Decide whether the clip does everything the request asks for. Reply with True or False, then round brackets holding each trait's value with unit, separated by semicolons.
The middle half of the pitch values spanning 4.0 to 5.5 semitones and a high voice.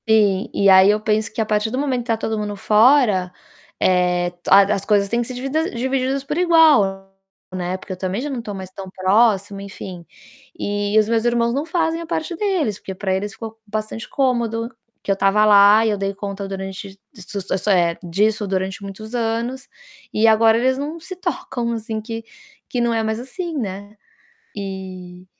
False (3.6 semitones; 215 Hz)